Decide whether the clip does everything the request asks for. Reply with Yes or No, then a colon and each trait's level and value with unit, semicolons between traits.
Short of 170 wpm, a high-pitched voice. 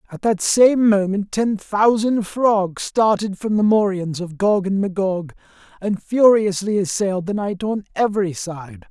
Yes: average, 155 wpm; high, 200 Hz